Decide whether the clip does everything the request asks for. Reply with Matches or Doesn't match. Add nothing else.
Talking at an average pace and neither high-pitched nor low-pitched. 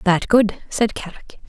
Doesn't match